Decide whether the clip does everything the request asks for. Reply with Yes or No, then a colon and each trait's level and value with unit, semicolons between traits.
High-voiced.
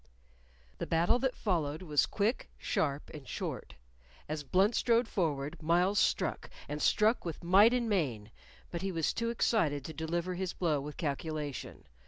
No: medium, 170 Hz